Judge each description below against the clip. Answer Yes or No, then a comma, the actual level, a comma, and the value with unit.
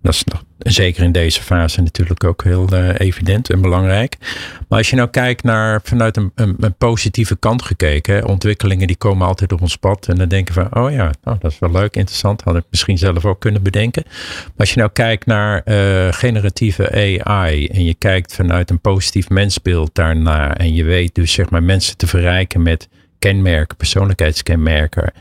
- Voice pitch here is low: Yes, very low, 95 Hz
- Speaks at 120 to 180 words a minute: No, average, 195 wpm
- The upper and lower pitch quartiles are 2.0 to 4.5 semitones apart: Yes, average, 2.8 semitones